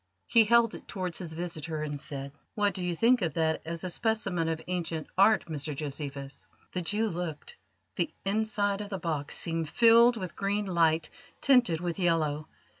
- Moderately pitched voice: Yes, medium, 175 Hz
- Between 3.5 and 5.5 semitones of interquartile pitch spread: Yes, average, 4.5 semitones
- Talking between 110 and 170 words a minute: No, average, 180 wpm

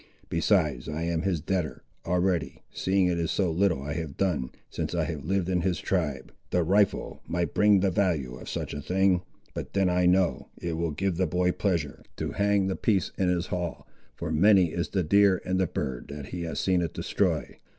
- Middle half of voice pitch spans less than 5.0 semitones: Yes, average, 2.9 semitones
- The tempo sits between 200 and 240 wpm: Yes, fast, 205 wpm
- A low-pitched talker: Yes, very low, 90 Hz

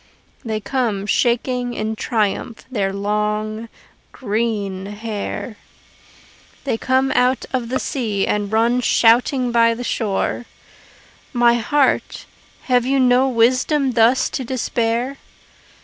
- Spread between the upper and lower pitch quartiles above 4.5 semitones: No, average, 2.8 semitones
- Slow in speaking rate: Yes, slow, 115 wpm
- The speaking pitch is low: No, high, 235 Hz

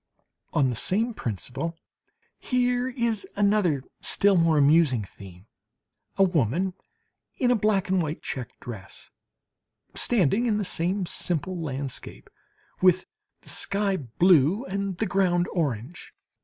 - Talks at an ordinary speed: No, slow, 125 wpm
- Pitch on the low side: No, medium, 180 Hz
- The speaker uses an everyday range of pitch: No, wide, 6.3 semitones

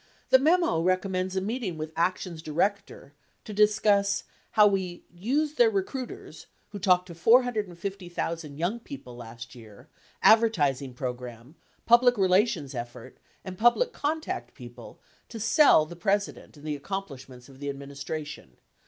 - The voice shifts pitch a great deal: Yes, wide, 7.1 semitones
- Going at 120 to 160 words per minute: Yes, slow, 135 wpm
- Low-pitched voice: No, medium, 185 Hz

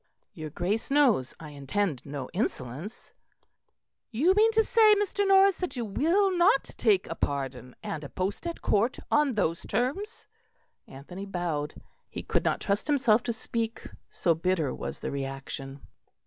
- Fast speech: No, average, 155 wpm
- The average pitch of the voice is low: No, high, 205 Hz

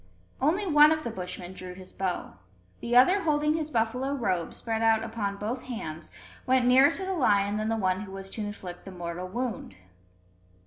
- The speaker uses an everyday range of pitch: No, wide, 5.8 semitones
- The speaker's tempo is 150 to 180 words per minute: No, average, 190 wpm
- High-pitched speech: Yes, high, 225 Hz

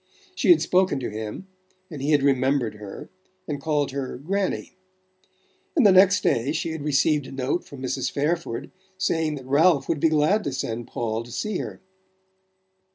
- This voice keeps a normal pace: Yes, average, 175 wpm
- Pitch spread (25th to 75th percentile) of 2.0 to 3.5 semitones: No, average, 4.0 semitones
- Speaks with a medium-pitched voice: Yes, medium, 145 Hz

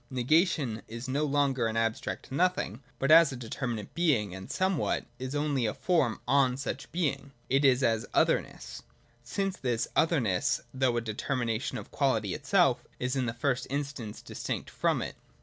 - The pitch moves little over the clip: No, average, 3.8 semitones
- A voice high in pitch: No, low, 130 Hz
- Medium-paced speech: Yes, average, 175 wpm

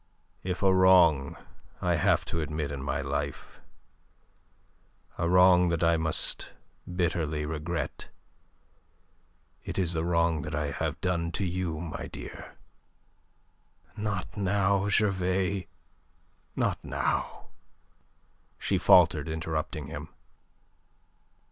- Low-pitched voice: Yes, very low, 85 Hz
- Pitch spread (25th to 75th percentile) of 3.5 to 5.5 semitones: No, average, 3.1 semitones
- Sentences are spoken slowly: Yes, slow, 105 wpm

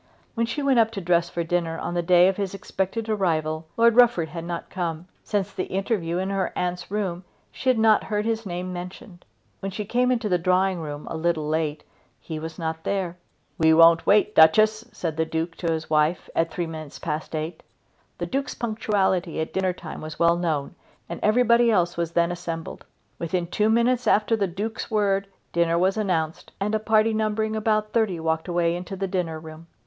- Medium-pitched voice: Yes, medium, 180 Hz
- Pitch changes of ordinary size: Yes, average, 4.3 semitones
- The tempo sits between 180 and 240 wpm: Yes, average, 200 wpm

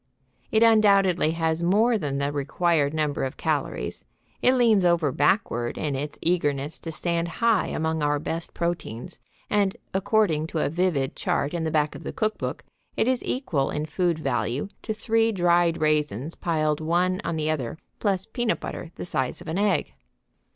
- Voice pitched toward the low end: No, medium, 165 Hz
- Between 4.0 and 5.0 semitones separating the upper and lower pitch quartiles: Yes, average, 4.5 semitones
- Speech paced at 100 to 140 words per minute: No, average, 170 wpm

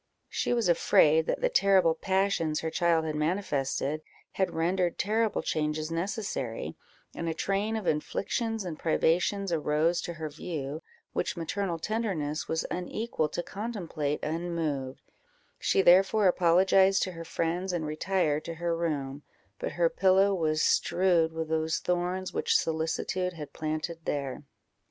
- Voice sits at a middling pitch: Yes, medium, 170 Hz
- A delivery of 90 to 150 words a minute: Yes, average, 140 wpm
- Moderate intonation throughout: Yes, average, 3.4 semitones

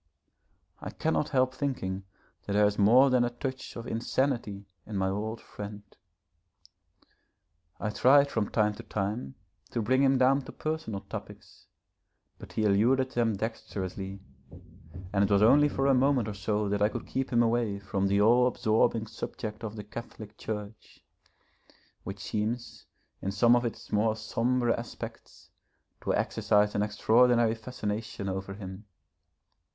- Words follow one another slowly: No, average, 150 wpm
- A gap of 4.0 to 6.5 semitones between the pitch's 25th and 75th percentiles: No, average, 3.2 semitones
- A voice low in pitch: Yes, low, 110 Hz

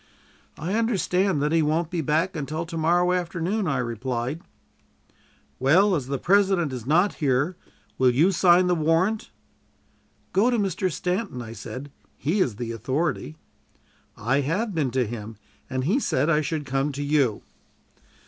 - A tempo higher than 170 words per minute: No, average, 160 wpm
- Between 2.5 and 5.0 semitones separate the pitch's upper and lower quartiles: No, wide, 5.5 semitones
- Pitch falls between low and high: Yes, medium, 155 Hz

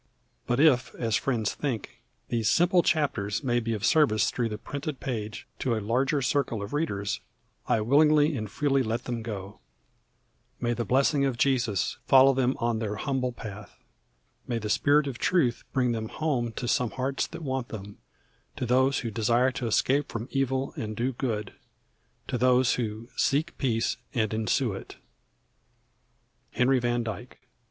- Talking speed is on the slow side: No, average, 165 wpm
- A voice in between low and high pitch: No, low, 125 Hz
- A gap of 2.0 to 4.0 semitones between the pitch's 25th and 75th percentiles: Yes, average, 3.5 semitones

